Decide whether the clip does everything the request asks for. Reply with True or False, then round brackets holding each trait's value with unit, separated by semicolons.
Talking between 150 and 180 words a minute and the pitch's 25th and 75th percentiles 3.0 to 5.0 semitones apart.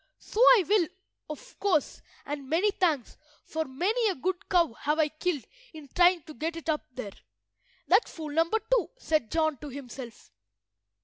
True (170 wpm; 4.0 semitones)